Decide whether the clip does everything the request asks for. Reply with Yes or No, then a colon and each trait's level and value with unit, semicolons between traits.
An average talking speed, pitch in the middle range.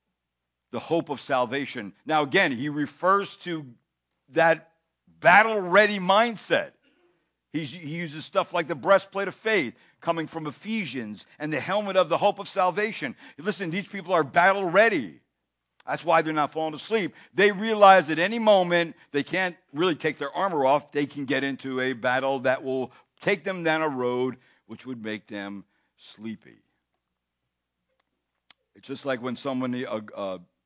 Yes: average, 160 wpm; medium, 155 Hz